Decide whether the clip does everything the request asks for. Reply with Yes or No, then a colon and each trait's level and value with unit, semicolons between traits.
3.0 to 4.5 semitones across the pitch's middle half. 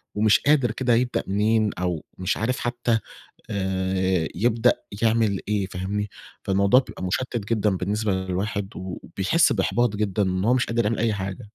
Yes: average, 3.5 semitones